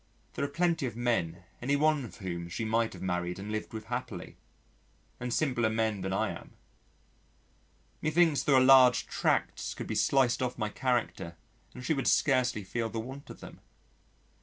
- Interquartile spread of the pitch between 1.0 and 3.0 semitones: No, average, 4.1 semitones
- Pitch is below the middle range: Yes, low, 120 Hz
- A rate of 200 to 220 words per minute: No, average, 180 wpm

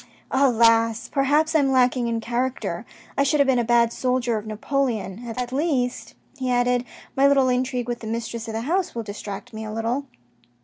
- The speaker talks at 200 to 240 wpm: Yes, fast, 205 wpm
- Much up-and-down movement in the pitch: No, average, 2.7 semitones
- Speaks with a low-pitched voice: No, high, 245 Hz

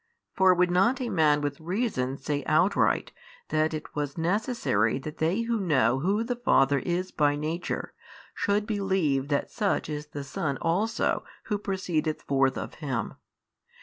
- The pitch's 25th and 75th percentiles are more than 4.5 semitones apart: Yes, wide, 5.4 semitones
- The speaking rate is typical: Yes, average, 155 wpm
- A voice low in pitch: No, medium, 160 Hz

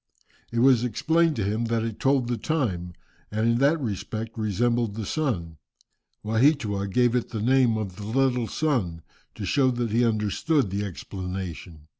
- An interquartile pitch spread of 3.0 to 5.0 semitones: Yes, average, 4.0 semitones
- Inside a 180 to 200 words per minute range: No, average, 165 wpm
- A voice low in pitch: Yes, low, 115 Hz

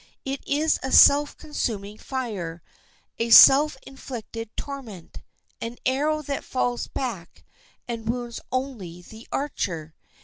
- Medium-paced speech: No, slow, 115 wpm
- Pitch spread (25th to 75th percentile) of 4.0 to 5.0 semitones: Yes, average, 4.4 semitones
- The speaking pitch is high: Yes, high, 245 Hz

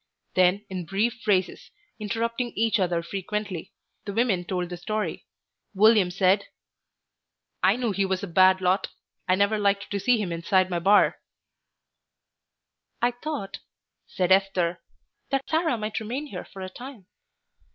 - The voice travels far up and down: No, average, 3.3 semitones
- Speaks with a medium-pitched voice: No, high, 200 Hz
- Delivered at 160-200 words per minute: No, average, 145 wpm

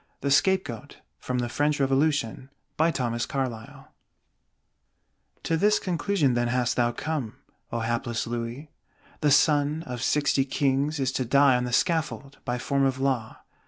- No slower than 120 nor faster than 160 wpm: Yes, slow, 135 wpm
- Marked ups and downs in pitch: No, average, 3.5 semitones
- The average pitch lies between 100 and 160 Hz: Yes, low, 135 Hz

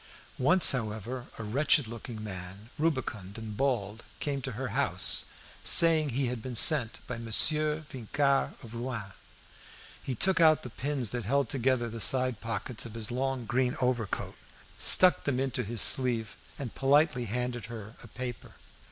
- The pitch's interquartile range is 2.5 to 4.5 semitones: Yes, average, 3.3 semitones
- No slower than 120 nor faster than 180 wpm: Yes, average, 160 wpm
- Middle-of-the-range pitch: No, low, 125 Hz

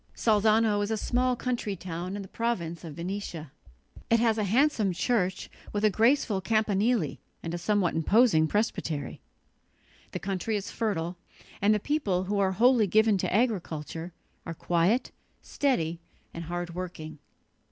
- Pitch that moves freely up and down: No, average, 4.5 semitones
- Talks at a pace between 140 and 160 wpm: Yes, average, 150 wpm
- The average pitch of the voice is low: No, high, 200 Hz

